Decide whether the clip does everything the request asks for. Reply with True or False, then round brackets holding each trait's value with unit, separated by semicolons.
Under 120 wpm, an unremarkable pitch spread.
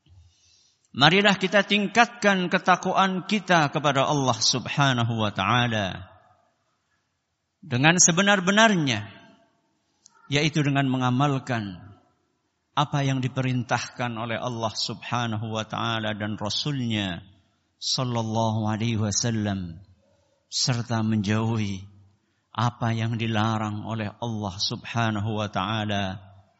True (85 wpm; 4.9 semitones)